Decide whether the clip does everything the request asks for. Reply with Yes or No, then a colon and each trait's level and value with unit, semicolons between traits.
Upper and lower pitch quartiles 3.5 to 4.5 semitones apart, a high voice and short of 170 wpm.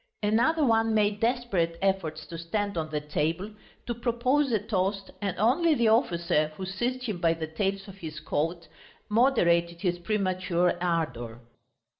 No: average, 4.9 semitones; high, 195 Hz; average, 155 wpm